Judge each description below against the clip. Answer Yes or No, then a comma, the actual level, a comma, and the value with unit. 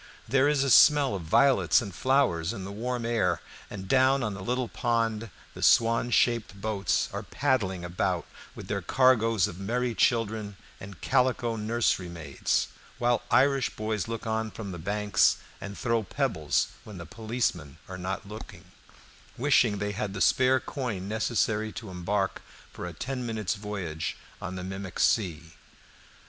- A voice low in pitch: Yes, low, 110 Hz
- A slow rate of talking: No, average, 160 wpm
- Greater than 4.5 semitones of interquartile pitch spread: No, average, 3.8 semitones